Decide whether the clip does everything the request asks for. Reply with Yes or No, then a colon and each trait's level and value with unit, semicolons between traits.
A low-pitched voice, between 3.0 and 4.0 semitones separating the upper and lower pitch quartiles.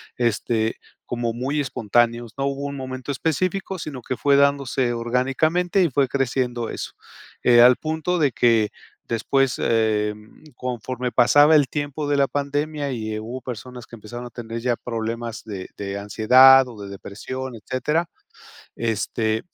Yes: low, 125 Hz; average, 3.4 semitones